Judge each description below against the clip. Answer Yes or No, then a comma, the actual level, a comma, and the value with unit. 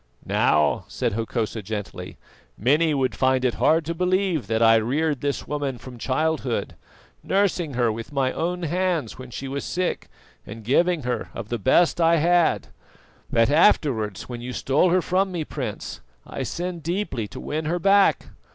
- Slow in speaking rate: No, average, 170 wpm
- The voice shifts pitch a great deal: Yes, wide, 6.1 semitones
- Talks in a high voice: No, medium, 145 Hz